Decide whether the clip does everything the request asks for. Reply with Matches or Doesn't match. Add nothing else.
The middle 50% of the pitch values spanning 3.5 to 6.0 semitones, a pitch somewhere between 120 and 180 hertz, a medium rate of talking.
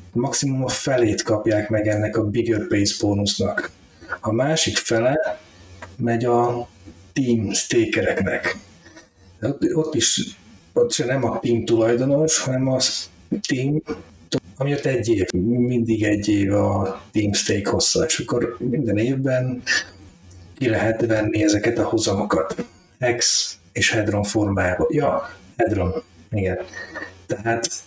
Doesn't match